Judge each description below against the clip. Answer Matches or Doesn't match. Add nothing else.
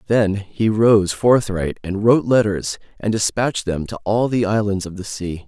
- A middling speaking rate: Matches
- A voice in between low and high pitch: Doesn't match